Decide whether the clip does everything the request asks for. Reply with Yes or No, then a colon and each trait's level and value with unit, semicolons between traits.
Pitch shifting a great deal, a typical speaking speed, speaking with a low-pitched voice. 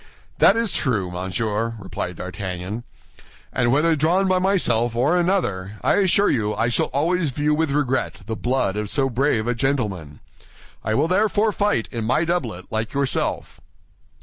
Yes: wide, 7.3 semitones; average, 160 wpm; low, 125 Hz